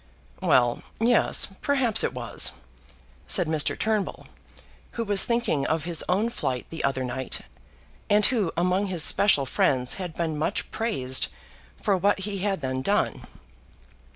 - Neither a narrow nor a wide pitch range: No, wide, 6.6 semitones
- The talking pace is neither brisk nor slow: Yes, average, 145 wpm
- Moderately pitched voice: Yes, medium, 180 Hz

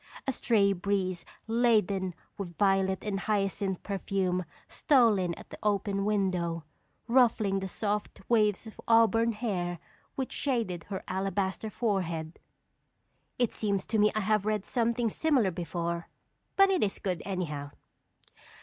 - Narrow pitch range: No, average, 3.2 semitones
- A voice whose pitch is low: No, high, 200 Hz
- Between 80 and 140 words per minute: Yes, slow, 135 wpm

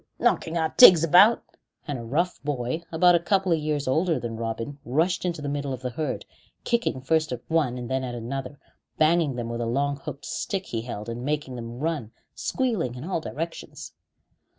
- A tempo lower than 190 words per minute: No, average, 195 wpm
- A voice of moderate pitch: Yes, medium, 145 Hz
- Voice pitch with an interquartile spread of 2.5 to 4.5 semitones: No, average, 5.1 semitones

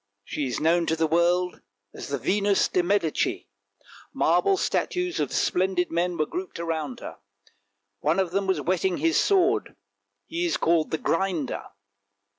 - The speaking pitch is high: No, medium, 180 Hz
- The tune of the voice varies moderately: Yes, average, 3.7 semitones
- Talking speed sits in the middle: Yes, average, 155 wpm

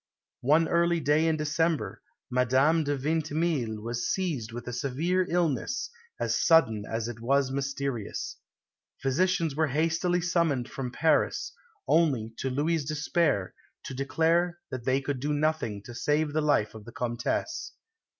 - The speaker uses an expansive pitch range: No, average, 4.6 semitones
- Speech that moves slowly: No, average, 145 wpm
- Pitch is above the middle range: No, medium, 145 Hz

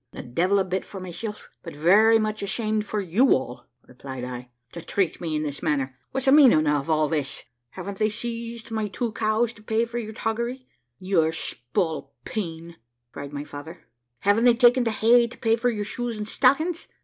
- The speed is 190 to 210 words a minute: Yes, average, 195 wpm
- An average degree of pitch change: No, wide, 6.5 semitones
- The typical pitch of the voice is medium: No, high, 210 Hz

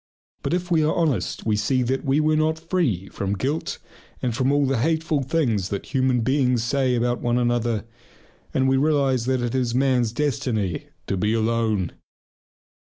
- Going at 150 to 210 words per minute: Yes, average, 175 wpm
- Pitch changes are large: No, average, 3.8 semitones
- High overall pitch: No, low, 130 Hz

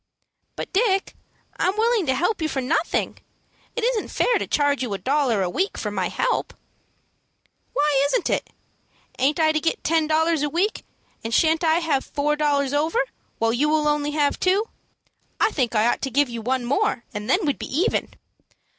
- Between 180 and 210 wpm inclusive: Yes, average, 190 wpm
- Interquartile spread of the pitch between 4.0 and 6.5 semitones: Yes, average, 4.4 semitones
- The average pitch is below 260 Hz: No, very high, 300 Hz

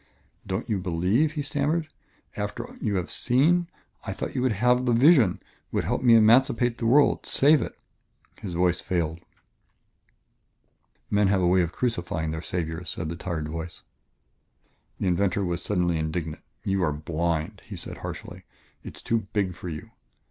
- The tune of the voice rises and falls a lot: Yes, wide, 6.1 semitones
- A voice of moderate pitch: No, very low, 95 Hz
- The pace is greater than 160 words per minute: Yes, average, 170 wpm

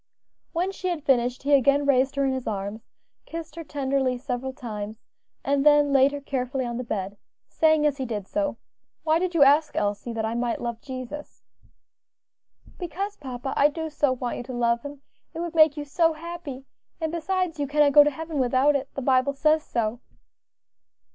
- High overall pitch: Yes, very high, 280 Hz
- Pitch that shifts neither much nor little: Yes, average, 3.6 semitones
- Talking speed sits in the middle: Yes, average, 195 wpm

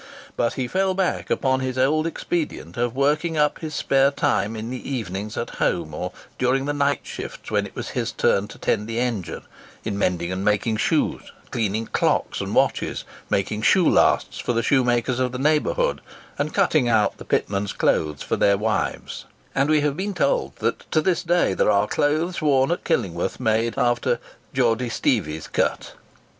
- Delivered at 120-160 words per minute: No, average, 185 wpm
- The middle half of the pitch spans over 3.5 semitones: Yes, wide, 5.5 semitones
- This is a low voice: Yes, low, 125 Hz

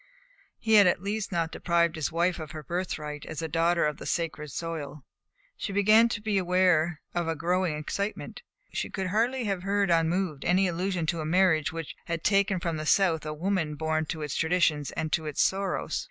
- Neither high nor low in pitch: Yes, medium, 170 Hz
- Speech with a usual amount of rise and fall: Yes, average, 3.3 semitones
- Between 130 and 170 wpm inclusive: No, average, 200 wpm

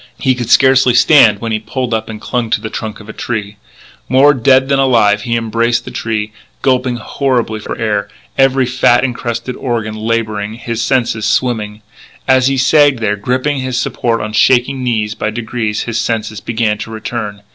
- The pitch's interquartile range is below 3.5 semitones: Yes, average, 2.9 semitones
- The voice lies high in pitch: No, low, 115 Hz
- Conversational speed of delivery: Yes, average, 180 wpm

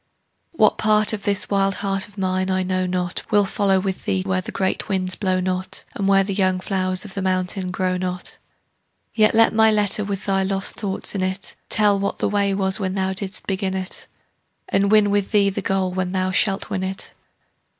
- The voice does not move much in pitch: Yes, narrow, 1.4 semitones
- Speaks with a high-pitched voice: Yes, high, 195 Hz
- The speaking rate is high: Yes, fast, 210 wpm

